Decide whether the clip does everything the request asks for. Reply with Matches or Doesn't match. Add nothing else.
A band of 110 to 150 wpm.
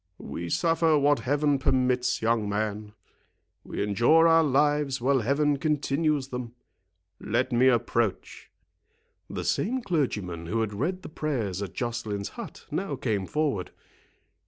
Matches